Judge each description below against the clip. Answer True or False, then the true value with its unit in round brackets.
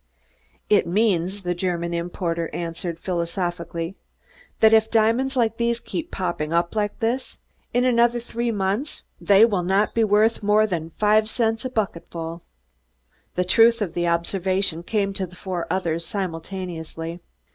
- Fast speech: False (150 wpm)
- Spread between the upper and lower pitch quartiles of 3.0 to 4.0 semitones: False (4.5 semitones)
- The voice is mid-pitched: False (195 Hz)